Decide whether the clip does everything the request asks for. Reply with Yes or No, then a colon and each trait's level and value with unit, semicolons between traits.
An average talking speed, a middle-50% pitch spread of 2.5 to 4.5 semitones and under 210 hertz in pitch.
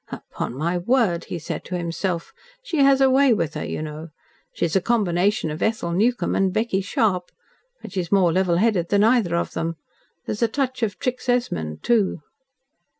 No: average, 195 wpm; wide, 5.5 semitones; high, 190 Hz